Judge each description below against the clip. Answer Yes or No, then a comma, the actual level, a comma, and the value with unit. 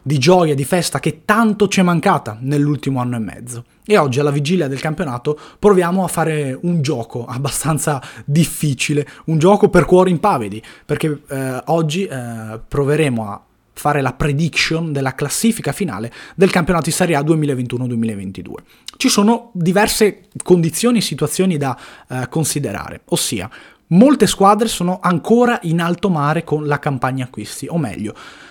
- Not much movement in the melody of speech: No, average, 5.3 semitones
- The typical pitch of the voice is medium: Yes, medium, 155 Hz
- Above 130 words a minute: Yes, average, 150 wpm